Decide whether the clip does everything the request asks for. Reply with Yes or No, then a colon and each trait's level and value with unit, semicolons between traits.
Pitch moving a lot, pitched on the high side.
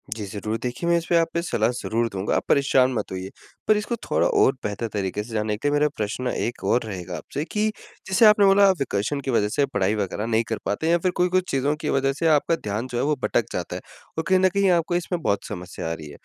No: wide, 8.2 semitones; low, 130 Hz